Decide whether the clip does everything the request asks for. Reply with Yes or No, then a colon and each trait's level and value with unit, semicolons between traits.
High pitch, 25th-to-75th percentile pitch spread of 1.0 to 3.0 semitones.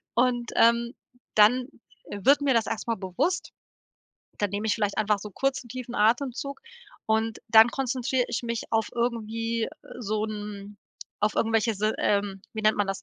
Yes: high, 225 Hz; narrow, 2.5 semitones